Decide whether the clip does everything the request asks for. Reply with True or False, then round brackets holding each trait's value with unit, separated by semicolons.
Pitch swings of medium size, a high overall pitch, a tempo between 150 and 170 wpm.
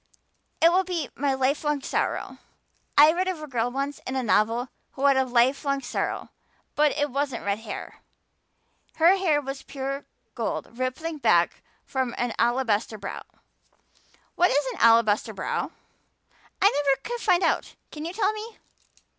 True (4.2 semitones; 275 Hz; 155 wpm)